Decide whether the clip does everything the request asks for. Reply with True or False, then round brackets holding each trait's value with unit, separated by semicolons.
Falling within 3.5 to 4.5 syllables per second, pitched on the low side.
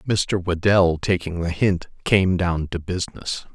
True (4.2 syllables/s; 90 Hz)